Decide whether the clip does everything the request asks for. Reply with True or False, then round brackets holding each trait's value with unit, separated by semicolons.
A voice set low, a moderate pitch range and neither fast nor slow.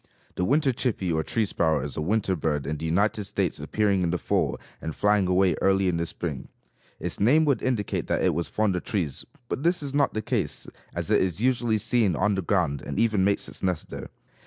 False (95 Hz; 4.8 semitones; 230 wpm)